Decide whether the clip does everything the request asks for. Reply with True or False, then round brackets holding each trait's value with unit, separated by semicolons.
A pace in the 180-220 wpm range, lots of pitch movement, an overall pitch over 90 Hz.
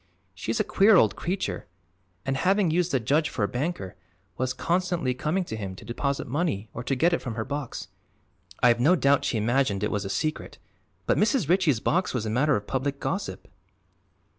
True (195 wpm; 6.8 semitones; 140 Hz)